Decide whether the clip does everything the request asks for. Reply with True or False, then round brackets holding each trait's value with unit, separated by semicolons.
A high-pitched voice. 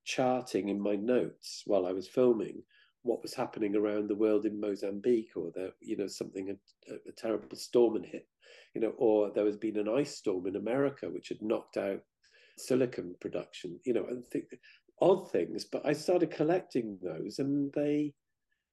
False (110 Hz)